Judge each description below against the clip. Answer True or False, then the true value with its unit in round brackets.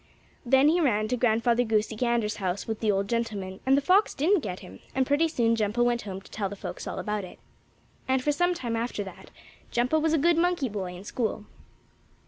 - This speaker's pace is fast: True (220 wpm)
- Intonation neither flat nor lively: True (4.9 semitones)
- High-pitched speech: True (235 Hz)